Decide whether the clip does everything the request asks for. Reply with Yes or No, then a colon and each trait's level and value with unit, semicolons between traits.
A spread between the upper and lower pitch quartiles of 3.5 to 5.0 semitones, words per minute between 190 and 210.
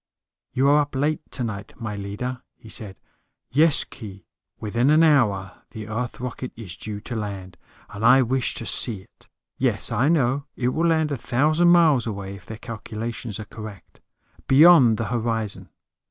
No: average, 4.6 semitones; average, 170 wpm